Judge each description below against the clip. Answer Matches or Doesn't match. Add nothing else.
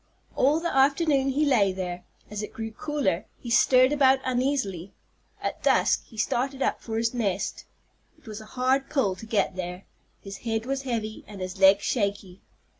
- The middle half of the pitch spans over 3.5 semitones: Matches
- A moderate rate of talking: Matches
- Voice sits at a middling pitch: Doesn't match